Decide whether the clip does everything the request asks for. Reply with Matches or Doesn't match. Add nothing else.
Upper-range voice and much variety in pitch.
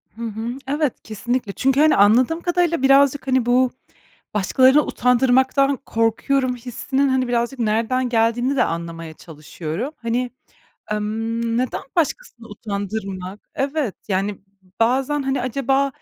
Doesn't match